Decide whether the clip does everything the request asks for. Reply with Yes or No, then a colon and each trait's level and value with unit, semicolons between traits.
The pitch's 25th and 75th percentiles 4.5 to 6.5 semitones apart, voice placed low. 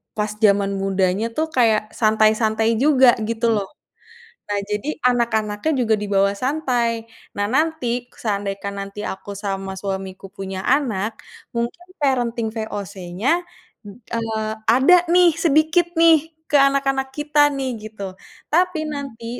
No: average, 5.2 semitones; high, 225 Hz